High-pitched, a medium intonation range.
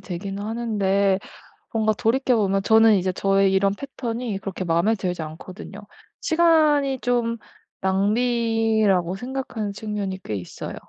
Yes: high, 210 Hz; average, 3.5 semitones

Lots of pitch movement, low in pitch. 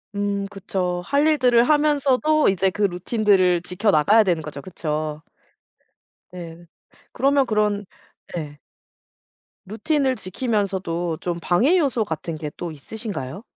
No: wide, 5.8 semitones; high, 195 Hz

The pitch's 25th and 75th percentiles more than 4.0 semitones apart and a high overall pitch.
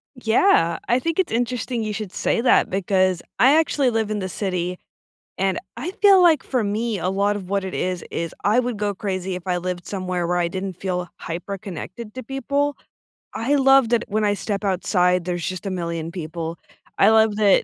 Yes: average, 4.5 semitones; high, 200 Hz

